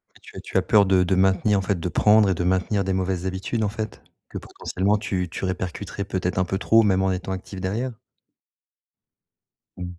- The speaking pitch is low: Yes, very low, 95 Hz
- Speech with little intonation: Yes, narrow, 1.7 semitones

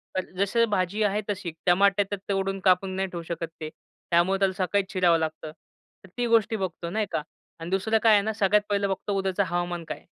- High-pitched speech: Yes, high, 195 Hz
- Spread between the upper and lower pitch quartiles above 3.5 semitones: No, narrow, 2.5 semitones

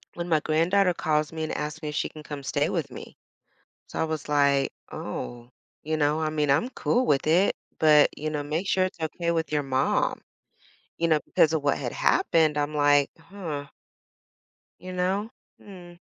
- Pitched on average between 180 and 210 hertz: No, medium, 155 Hz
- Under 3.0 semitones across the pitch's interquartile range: Yes, narrow, 2.6 semitones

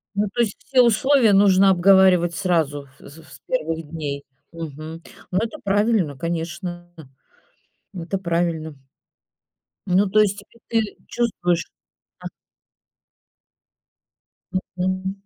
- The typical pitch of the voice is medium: Yes, medium, 180 Hz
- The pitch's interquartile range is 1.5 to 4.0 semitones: Yes, average, 3.7 semitones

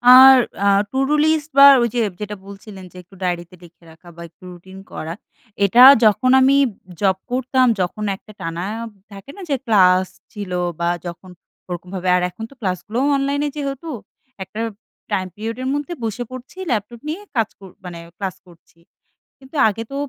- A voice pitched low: No, high, 210 Hz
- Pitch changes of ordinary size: No, wide, 6.0 semitones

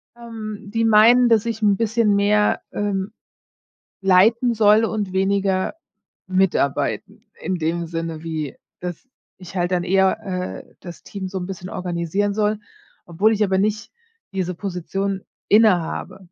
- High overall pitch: Yes, high, 195 Hz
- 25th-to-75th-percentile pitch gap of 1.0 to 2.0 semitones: No, average, 2.8 semitones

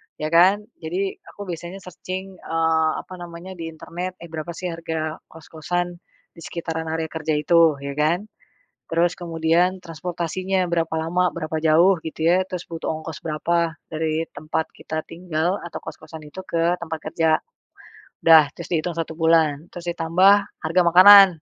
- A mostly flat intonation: Yes, narrow, 1.8 semitones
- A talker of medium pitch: Yes, medium, 165 Hz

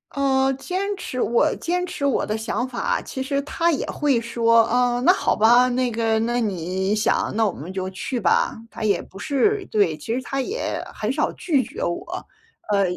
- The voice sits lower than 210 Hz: No, high, 245 Hz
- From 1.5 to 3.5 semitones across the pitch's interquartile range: No, average, 4.3 semitones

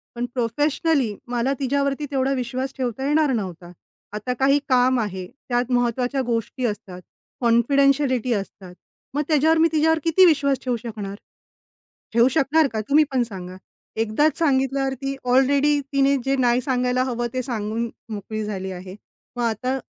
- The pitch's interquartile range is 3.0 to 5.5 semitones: Yes, average, 3.4 semitones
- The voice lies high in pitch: Yes, very high, 255 Hz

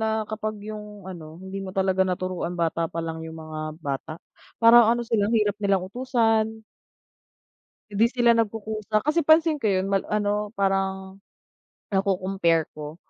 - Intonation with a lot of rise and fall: No, average, 3.1 semitones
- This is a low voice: No, high, 200 Hz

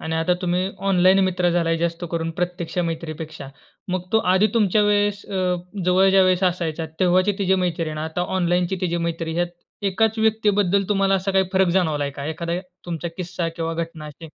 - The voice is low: No, medium, 180 Hz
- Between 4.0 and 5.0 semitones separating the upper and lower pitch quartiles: No, narrow, 2.6 semitones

